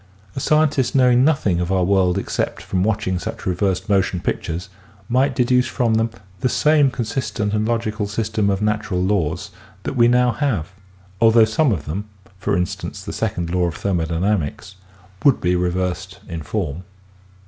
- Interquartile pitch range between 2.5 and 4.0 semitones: No, average, 4.7 semitones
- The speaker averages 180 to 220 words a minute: No, average, 165 wpm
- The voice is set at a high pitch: No, low, 100 Hz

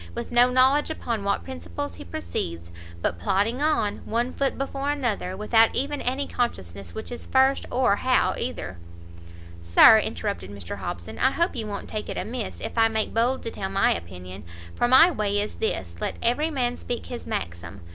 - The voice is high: Yes, high, 220 Hz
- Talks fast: No, average, 185 wpm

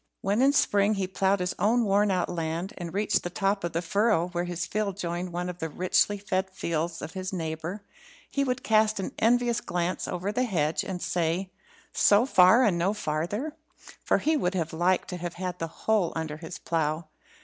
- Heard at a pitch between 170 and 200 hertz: Yes, medium, 185 Hz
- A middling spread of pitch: Yes, average, 3.3 semitones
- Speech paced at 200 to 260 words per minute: Yes, fast, 205 wpm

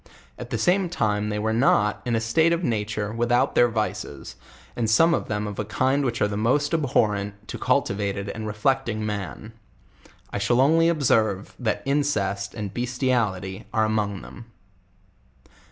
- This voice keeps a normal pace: Yes, average, 165 wpm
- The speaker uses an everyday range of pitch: Yes, average, 3.8 semitones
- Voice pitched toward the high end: No, low, 110 Hz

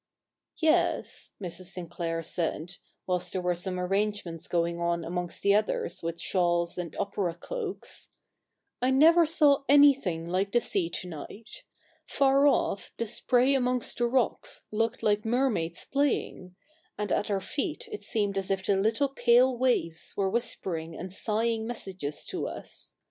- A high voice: Yes, high, 200 Hz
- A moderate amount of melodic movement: No, wide, 6.1 semitones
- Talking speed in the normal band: Yes, average, 160 wpm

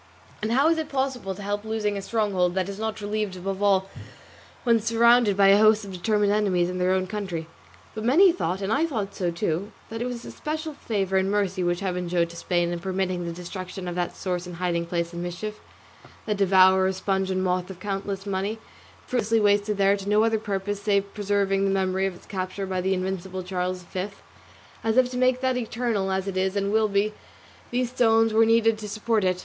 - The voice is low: No, high, 195 Hz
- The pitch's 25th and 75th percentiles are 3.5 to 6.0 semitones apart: No, average, 2.8 semitones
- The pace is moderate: No, fast, 215 wpm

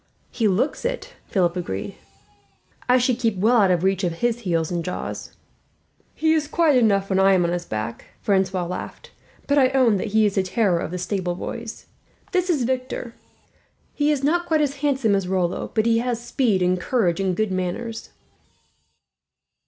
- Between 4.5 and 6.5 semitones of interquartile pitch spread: Yes, wide, 5.6 semitones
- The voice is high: Yes, high, 215 Hz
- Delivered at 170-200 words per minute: Yes, average, 185 wpm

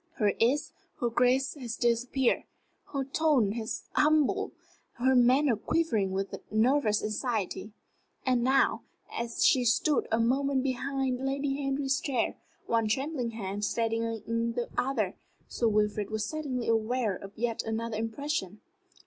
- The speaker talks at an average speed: No, slow, 130 wpm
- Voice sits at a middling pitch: No, high, 240 Hz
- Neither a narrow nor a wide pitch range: Yes, average, 3.4 semitones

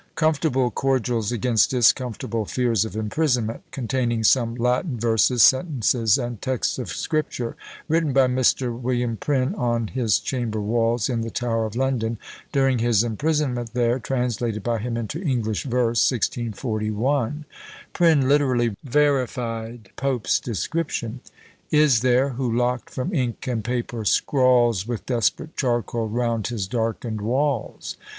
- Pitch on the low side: Yes, low, 120 Hz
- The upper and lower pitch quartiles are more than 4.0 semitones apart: No, narrow, 2.5 semitones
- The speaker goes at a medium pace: No, slow, 130 wpm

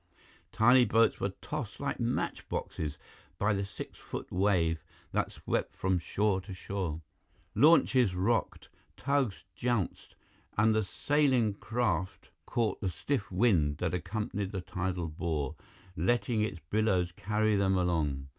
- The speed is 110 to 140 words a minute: Yes, slow, 135 wpm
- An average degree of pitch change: Yes, average, 4.1 semitones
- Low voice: Yes, low, 100 Hz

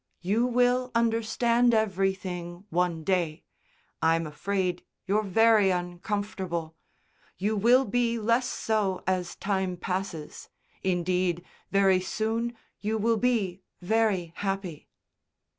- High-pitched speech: Yes, high, 195 Hz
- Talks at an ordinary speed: No, slow, 105 wpm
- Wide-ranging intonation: No, average, 3.9 semitones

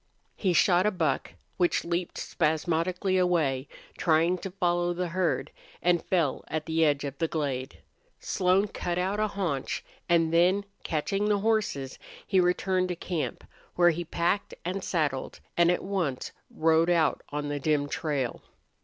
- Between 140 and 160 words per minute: Yes, average, 155 wpm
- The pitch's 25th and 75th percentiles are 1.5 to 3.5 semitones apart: Yes, average, 2.9 semitones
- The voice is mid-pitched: Yes, medium, 175 Hz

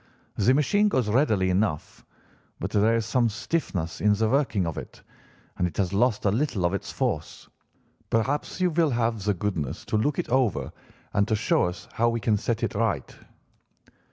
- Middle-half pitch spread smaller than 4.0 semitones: No, average, 4.5 semitones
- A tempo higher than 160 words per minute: Yes, average, 185 wpm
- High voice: No, low, 110 Hz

